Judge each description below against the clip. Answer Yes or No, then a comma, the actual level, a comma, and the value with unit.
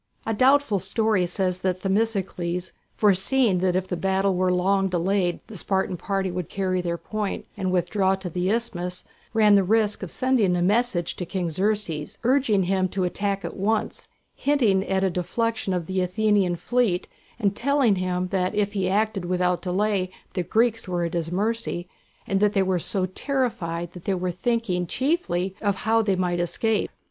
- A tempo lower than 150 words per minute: No, average, 180 wpm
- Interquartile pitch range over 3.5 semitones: No, average, 3.0 semitones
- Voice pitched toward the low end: No, high, 190 Hz